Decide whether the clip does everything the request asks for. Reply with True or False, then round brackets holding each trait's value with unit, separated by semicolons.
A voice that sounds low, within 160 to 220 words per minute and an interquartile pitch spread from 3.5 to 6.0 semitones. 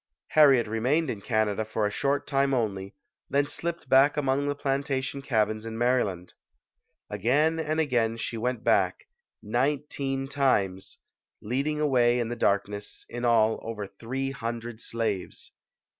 False (120 Hz; 145 wpm; 4.0 semitones)